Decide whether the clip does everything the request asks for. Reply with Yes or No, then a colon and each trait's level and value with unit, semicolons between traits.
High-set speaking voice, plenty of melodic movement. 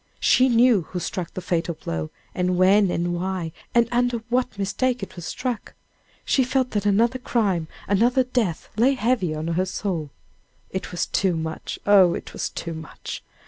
Yes: high, 195 Hz; wide, 5.7 semitones